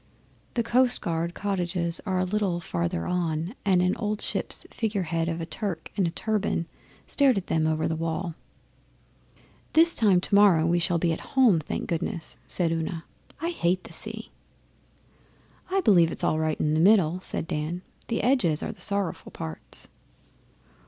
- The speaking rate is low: No, average, 165 wpm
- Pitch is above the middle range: No, medium, 175 Hz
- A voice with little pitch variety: No, average, 4.0 semitones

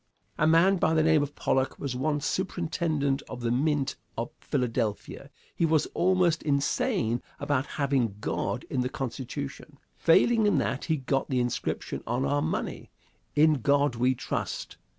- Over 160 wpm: No, average, 155 wpm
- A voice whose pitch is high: No, medium, 145 Hz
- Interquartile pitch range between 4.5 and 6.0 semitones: No, average, 3.6 semitones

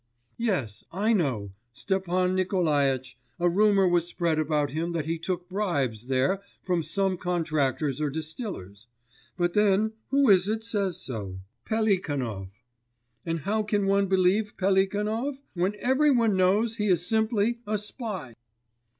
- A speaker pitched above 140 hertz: Yes, medium, 185 Hz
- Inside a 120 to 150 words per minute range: Yes, average, 140 wpm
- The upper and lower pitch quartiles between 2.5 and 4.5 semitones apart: No, average, 5.3 semitones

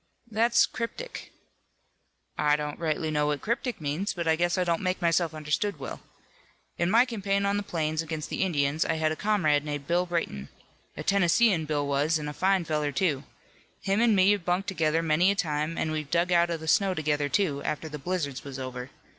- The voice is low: No, medium, 165 Hz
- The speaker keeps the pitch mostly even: No, average, 4.2 semitones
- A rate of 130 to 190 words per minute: No, fast, 205 wpm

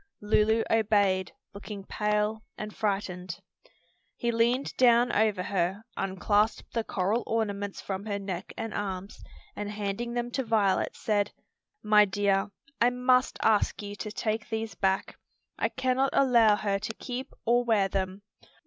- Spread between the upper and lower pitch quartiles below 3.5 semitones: Yes, narrow, 2.4 semitones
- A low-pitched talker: No, high, 210 Hz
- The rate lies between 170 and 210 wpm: No, average, 145 wpm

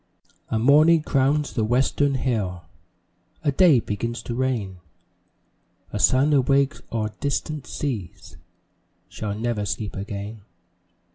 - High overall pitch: No, low, 125 Hz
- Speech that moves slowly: Yes, slow, 115 wpm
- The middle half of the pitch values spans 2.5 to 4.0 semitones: No, average, 4.8 semitones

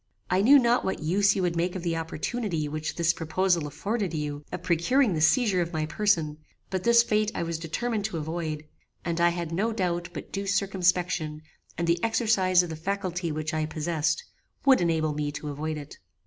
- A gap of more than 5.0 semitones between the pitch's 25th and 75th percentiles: No, average, 4.0 semitones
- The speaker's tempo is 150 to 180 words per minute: No, average, 200 wpm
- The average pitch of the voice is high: No, medium, 170 Hz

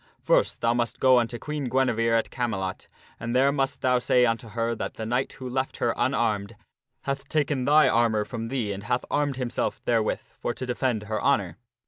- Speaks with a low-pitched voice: Yes, low, 120 Hz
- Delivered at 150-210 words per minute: Yes, average, 195 wpm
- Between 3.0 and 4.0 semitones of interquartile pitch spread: No, narrow, 2.6 semitones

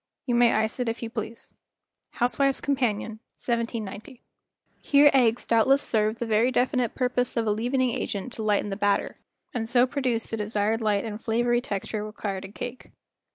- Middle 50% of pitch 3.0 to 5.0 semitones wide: No, narrow, 2.6 semitones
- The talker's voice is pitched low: No, high, 230 Hz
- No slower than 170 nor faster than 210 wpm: Yes, average, 180 wpm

